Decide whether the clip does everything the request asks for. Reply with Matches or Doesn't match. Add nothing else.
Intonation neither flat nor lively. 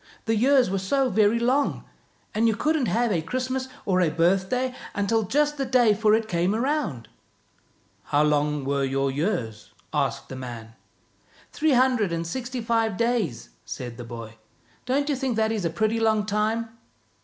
Doesn't match